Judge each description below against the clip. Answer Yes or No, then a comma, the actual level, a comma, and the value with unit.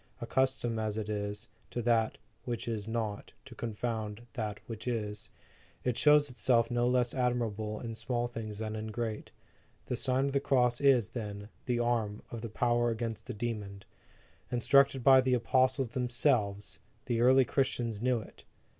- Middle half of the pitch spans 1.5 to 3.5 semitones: Yes, narrow, 2.4 semitones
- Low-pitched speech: Yes, low, 120 Hz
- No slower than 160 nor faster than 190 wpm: Yes, average, 165 wpm